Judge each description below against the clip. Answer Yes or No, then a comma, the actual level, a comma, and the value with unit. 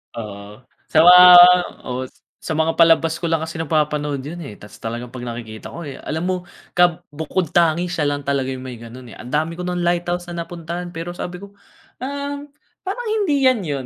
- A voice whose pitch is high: No, medium, 165 Hz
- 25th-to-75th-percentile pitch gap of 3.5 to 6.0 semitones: Yes, average, 4.1 semitones